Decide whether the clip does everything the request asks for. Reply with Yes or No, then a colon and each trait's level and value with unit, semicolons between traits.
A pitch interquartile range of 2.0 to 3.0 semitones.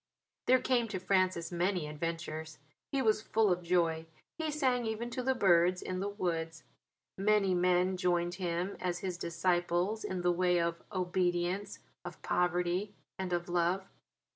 Yes: narrow, 2.5 semitones